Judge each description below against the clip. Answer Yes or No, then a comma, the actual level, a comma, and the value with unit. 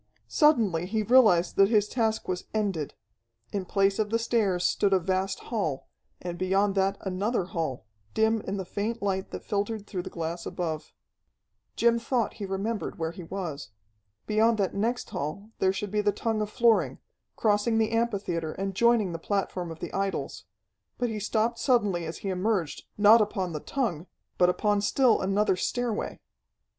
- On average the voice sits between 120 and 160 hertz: No, high, 200 Hz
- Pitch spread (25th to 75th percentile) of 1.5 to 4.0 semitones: Yes, average, 3.4 semitones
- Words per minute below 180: Yes, average, 170 wpm